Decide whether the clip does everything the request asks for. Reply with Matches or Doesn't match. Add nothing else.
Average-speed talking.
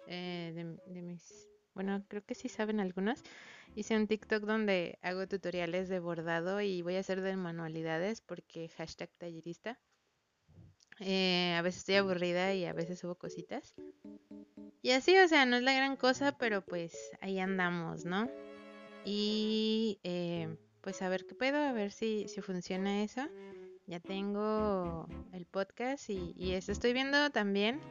Matches